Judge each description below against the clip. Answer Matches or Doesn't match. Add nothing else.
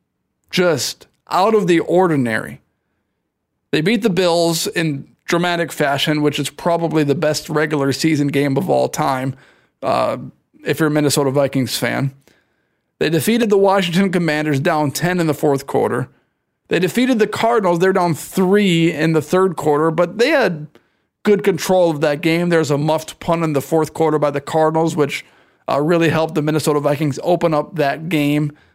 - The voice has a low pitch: Doesn't match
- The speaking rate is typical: Matches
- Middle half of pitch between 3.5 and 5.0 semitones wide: Doesn't match